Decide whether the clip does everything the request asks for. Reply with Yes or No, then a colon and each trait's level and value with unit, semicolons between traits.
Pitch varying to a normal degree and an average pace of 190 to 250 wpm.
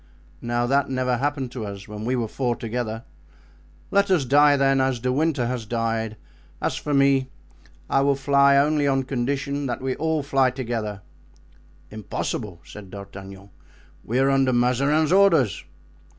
No: average, 3.4 semitones; average, 155 wpm